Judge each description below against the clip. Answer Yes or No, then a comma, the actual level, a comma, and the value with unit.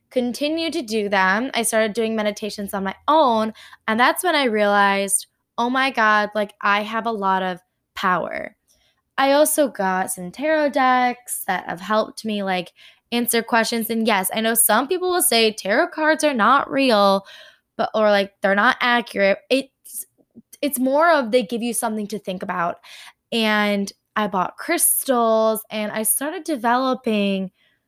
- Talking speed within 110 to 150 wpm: No, average, 165 wpm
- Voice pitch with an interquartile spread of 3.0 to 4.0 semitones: No, average, 4.4 semitones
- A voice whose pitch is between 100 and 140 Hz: No, high, 225 Hz